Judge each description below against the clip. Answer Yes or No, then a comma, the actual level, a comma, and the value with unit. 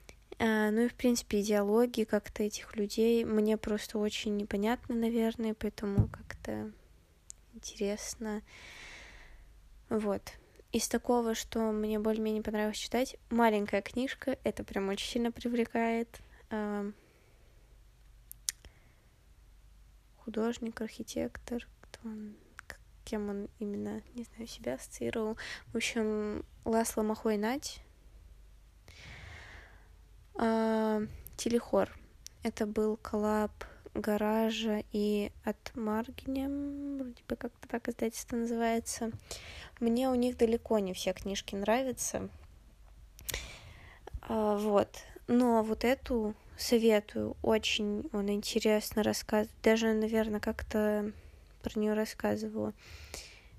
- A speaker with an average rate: No, slow, 95 wpm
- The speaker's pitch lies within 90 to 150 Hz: No, high, 220 Hz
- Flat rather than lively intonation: Yes, narrow, 1.9 semitones